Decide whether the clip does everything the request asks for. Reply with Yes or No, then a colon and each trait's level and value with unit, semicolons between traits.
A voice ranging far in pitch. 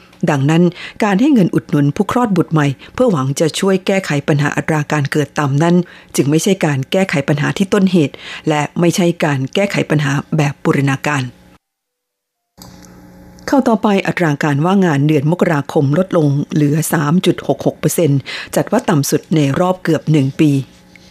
No: average, 3.8 semitones